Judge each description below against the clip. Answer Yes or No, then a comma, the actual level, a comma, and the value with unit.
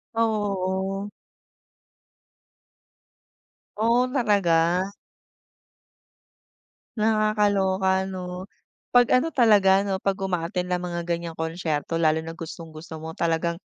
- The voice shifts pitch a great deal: No, average, 3.5 semitones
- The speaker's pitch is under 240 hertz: Yes, high, 190 Hz